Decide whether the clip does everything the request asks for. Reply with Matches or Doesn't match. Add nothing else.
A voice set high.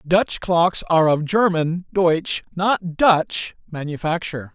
Doesn't match